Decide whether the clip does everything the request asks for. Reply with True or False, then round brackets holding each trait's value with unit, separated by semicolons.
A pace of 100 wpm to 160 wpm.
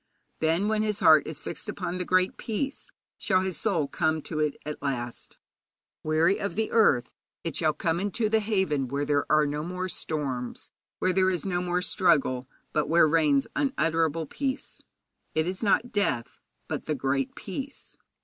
False (175 wpm)